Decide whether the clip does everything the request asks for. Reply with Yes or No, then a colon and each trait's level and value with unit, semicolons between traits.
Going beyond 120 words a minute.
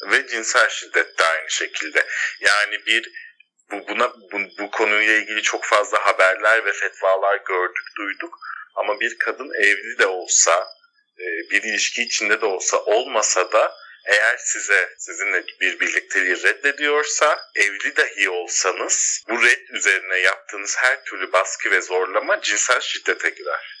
Yes: fast, 140 wpm